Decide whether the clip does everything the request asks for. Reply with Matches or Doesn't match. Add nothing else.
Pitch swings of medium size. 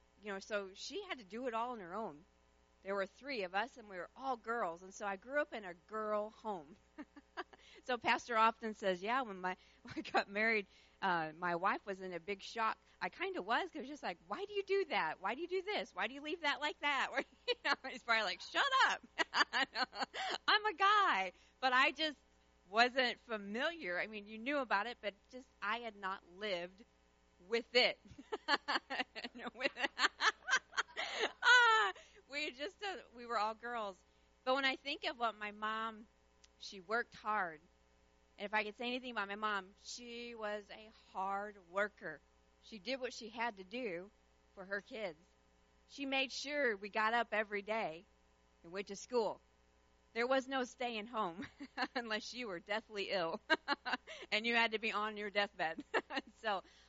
Matches